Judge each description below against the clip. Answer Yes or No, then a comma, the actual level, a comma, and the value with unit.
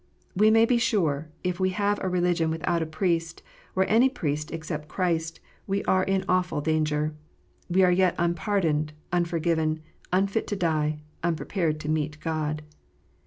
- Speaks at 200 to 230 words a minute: No, average, 155 wpm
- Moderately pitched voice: Yes, medium, 170 Hz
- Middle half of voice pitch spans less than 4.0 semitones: Yes, average, 3.3 semitones